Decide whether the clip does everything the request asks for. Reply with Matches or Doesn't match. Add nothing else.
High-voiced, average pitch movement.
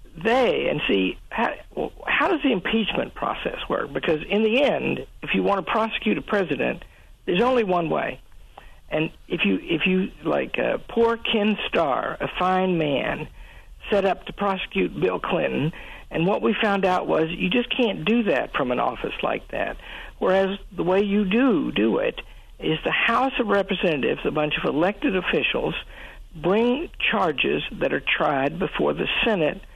Matches